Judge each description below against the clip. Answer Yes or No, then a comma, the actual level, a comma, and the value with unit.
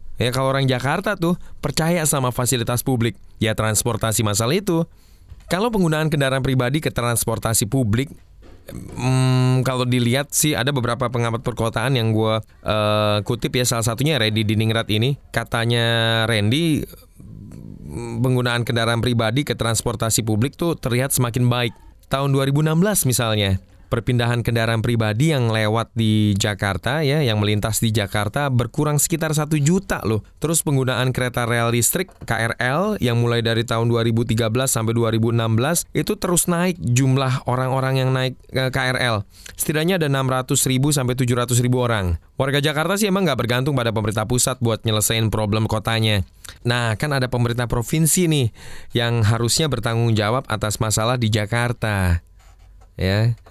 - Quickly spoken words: Yes, fast, 145 wpm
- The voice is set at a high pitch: No, low, 120 Hz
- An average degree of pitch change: Yes, average, 3.2 semitones